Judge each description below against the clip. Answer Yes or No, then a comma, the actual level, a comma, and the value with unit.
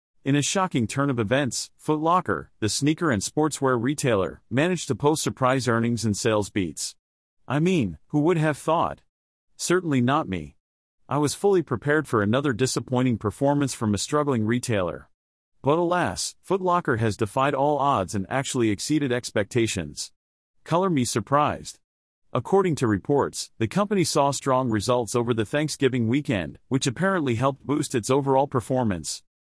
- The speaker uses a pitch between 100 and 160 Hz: Yes, low, 135 Hz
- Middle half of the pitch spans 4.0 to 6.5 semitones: Yes, average, 4.7 semitones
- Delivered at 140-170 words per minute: Yes, average, 150 wpm